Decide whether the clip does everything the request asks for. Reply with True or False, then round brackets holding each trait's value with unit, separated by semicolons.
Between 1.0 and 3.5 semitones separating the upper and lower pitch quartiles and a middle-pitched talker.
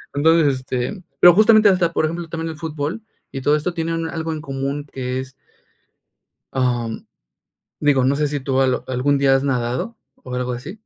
False (4.0 semitones; 145 Hz)